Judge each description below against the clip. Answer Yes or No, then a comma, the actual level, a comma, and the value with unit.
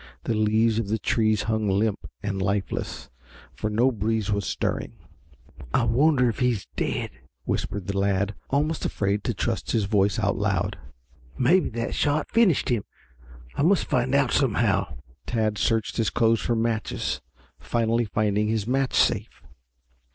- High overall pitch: No, low, 110 Hz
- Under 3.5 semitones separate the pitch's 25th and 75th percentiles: Yes, average, 2.9 semitones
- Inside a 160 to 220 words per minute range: No, average, 150 wpm